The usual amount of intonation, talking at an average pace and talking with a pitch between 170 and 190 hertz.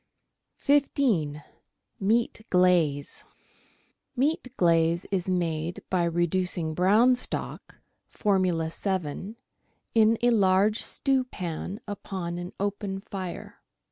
No: average, 3.9 semitones; slow, 90 wpm; medium, 185 Hz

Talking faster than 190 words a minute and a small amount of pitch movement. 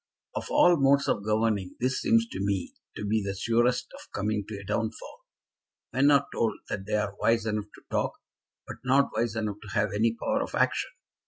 Yes: average, 200 wpm; narrow, 2.2 semitones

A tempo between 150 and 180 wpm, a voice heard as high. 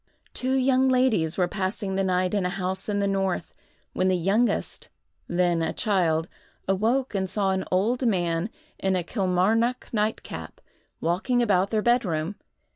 Yes: average, 160 wpm; high, 195 Hz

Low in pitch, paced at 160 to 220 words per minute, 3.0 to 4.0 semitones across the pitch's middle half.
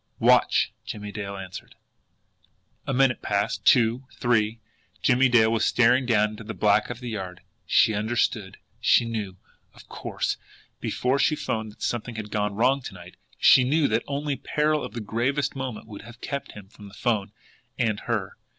Yes: low, 115 Hz; average, 175 wpm; average, 3.3 semitones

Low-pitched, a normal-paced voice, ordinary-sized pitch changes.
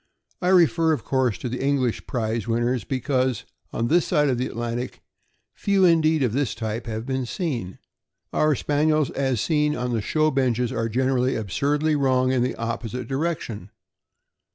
Yes: low, 130 Hz; average, 165 wpm; average, 4.0 semitones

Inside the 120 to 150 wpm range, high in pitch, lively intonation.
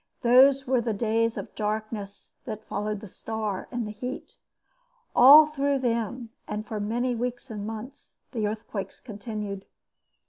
No: average, 145 wpm; high, 225 Hz; average, 2.8 semitones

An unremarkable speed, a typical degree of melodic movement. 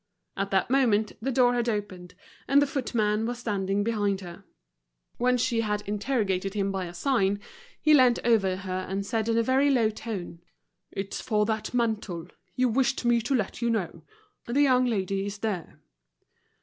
Yes: average, 175 wpm; average, 3.7 semitones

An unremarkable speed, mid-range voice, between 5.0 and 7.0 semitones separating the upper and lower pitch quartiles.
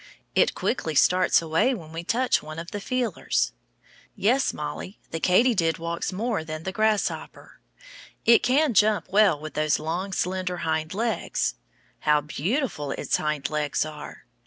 Yes: average, 150 wpm; medium, 180 Hz; wide, 5.6 semitones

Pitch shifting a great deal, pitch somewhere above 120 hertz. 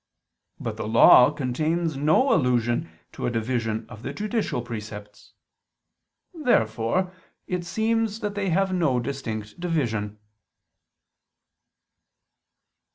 Yes: wide, 8.3 semitones; medium, 140 Hz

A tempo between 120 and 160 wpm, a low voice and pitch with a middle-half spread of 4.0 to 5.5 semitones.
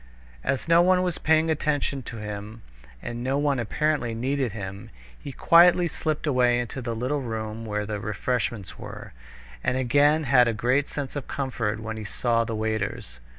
No: average, 180 wpm; low, 125 Hz; average, 4.6 semitones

